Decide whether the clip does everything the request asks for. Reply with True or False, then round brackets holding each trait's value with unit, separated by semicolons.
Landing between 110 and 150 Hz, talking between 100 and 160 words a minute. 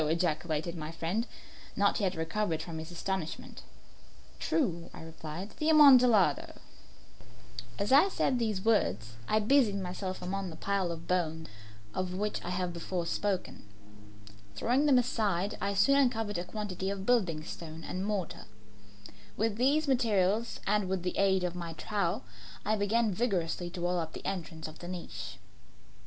False (190 Hz; 155 wpm)